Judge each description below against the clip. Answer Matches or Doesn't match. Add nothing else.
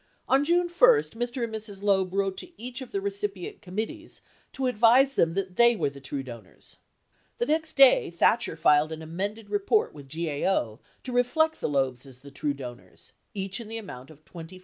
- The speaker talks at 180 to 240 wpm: Matches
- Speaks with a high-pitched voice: Matches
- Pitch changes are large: Matches